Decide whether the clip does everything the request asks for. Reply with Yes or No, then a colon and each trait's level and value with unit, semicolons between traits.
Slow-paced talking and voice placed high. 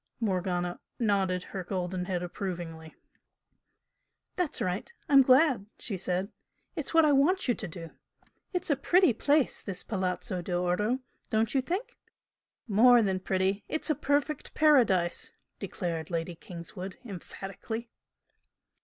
Yes: slow, 125 wpm; high, 195 Hz